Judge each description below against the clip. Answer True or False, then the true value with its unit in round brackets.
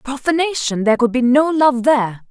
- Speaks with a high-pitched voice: True (265 Hz)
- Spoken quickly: False (180 wpm)